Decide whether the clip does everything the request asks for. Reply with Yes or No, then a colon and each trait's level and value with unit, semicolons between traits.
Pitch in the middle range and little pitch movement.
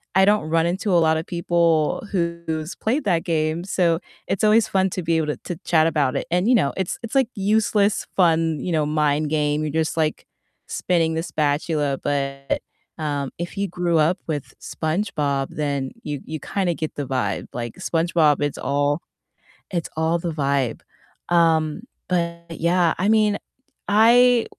No: medium, 165 Hz; average, 3.2 semitones